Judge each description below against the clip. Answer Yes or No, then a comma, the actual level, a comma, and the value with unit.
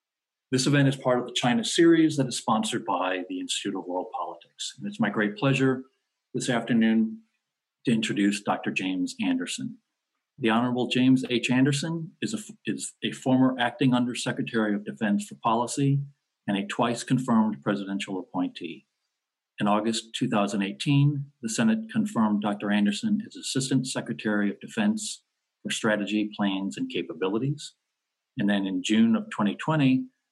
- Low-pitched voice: Yes, low, 130 Hz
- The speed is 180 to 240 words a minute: No, average, 145 wpm